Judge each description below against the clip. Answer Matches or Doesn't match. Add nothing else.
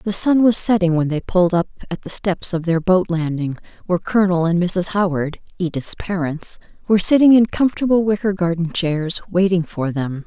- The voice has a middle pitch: Matches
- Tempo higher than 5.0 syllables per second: Matches